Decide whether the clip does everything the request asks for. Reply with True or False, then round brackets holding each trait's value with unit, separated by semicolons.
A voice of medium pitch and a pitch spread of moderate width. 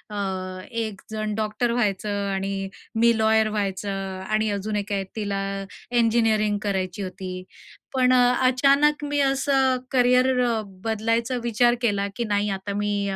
False (215 Hz; 3.2 semitones)